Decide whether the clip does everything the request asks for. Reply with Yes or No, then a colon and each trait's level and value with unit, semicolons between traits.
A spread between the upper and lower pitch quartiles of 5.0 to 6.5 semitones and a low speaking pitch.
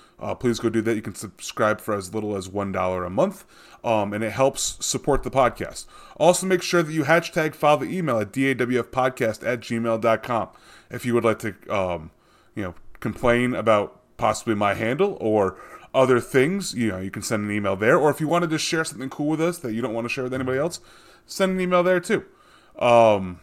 Yes: wide, 5.6 semitones; low, 120 Hz